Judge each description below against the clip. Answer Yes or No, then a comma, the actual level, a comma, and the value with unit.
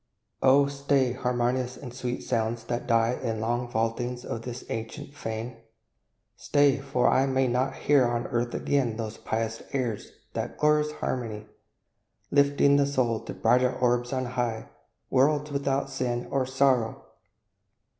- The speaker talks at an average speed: Yes, average, 145 wpm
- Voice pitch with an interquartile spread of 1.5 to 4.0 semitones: Yes, narrow, 2.6 semitones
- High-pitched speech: No, low, 125 Hz